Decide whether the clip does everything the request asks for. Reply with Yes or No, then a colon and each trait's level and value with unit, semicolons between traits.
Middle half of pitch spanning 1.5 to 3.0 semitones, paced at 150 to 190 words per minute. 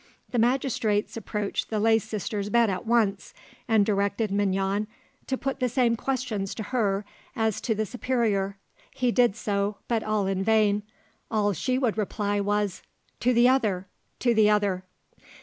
Yes: average, 2.7 semitones; average, 160 wpm